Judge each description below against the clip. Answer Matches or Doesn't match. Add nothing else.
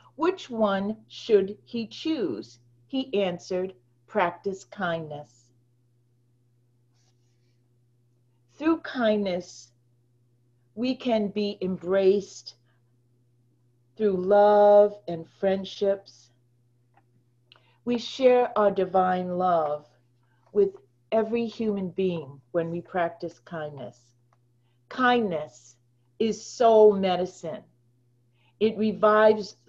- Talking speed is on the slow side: Matches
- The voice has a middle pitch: Matches